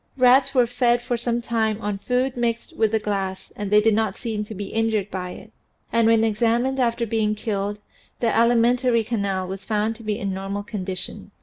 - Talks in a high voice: Yes, high, 220 Hz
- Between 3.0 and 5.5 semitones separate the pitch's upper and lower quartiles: No, narrow, 2.6 semitones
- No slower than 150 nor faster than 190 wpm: No, average, 200 wpm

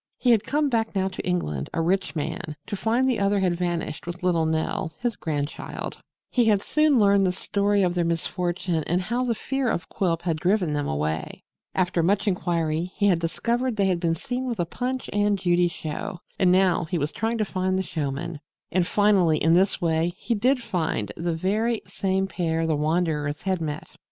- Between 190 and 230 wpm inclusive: Yes, average, 200 wpm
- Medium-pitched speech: Yes, medium, 180 Hz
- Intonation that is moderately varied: Yes, average, 3.9 semitones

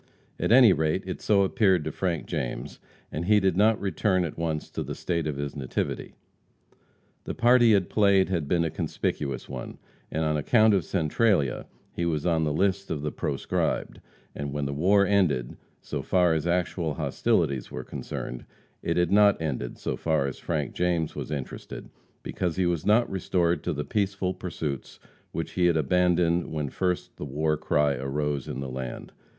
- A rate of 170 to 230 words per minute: Yes, average, 185 wpm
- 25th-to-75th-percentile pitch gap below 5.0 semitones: Yes, average, 4.4 semitones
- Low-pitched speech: Yes, very low, 85 Hz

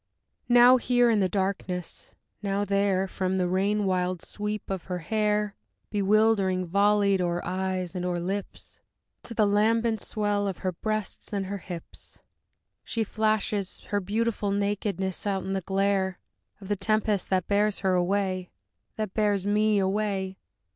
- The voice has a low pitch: No, high, 200 Hz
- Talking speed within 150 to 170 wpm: Yes, average, 155 wpm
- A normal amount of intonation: No, narrow, 1.9 semitones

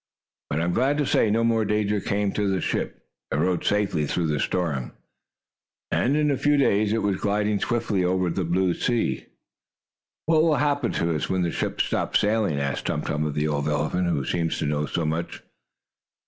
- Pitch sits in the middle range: No, very low, 95 Hz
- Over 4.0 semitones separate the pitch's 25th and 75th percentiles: Yes, wide, 5.5 semitones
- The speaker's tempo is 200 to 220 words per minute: Yes, fast, 205 wpm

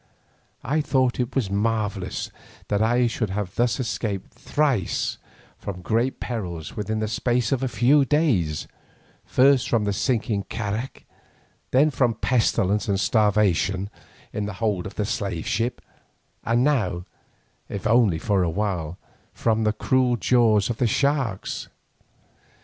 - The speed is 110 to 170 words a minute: Yes, average, 140 wpm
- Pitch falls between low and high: No, low, 110 Hz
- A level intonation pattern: No, average, 3.7 semitones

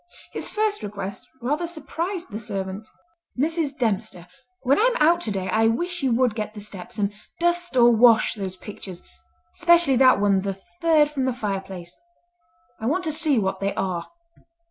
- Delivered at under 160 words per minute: No, average, 165 wpm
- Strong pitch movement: Yes, wide, 8.7 semitones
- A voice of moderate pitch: No, high, 245 Hz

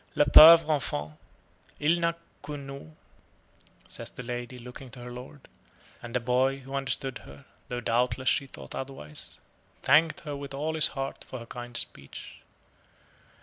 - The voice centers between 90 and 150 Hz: Yes, low, 135 Hz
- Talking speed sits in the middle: Yes, average, 155 wpm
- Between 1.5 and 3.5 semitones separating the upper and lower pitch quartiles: Yes, average, 3.0 semitones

